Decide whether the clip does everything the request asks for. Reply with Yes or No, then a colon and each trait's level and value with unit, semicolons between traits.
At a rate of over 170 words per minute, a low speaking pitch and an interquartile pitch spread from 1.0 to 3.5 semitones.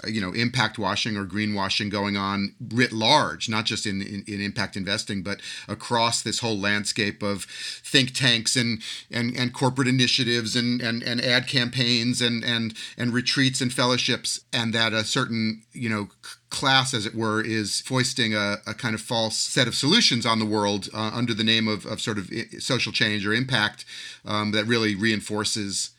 Yes: average, 180 wpm; low, 115 Hz; narrow, 2.6 semitones